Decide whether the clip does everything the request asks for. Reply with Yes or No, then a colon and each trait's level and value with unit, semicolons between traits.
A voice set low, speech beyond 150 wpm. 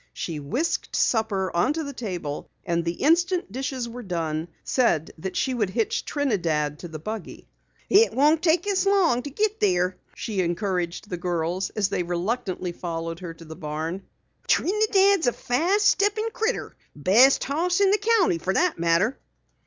No: high, 215 Hz; average, 165 wpm